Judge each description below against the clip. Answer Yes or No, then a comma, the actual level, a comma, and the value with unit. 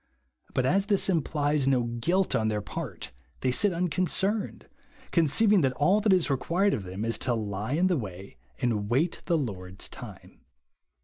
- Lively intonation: Yes, wide, 8.5 semitones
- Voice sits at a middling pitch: Yes, medium, 145 Hz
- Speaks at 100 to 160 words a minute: No, average, 175 wpm